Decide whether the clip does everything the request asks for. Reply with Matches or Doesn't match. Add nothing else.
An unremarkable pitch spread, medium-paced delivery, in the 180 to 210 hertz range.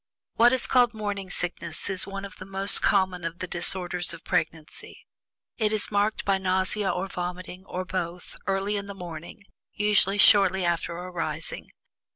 Doesn't match